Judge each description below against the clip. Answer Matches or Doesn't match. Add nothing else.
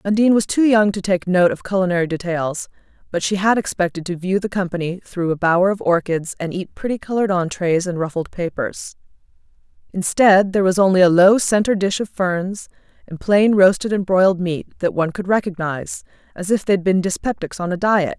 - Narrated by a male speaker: Doesn't match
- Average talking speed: Matches